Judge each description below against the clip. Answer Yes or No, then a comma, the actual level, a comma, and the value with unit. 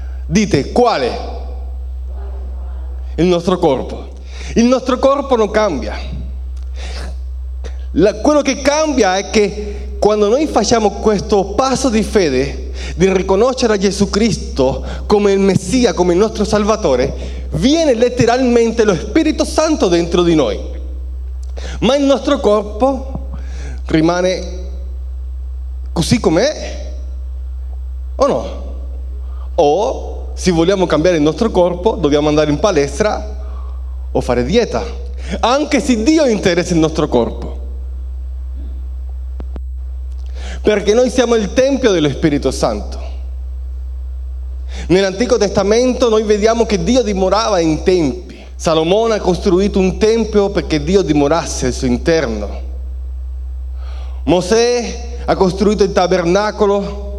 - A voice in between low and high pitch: Yes, medium, 155 Hz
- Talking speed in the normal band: No, slow, 110 wpm